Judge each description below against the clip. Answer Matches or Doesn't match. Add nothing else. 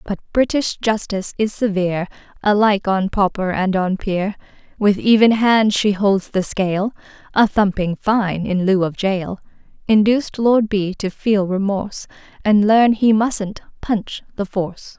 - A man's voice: Doesn't match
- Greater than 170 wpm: Doesn't match